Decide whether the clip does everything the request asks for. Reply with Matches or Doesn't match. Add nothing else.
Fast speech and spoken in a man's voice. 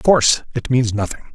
Matches